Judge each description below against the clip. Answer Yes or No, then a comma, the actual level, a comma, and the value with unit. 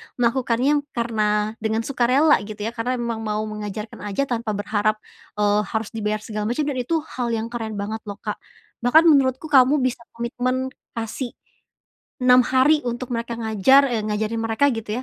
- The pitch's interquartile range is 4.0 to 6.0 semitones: No, average, 3.0 semitones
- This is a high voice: Yes, high, 230 Hz